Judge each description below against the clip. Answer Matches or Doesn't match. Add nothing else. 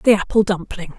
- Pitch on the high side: Matches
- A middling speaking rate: Matches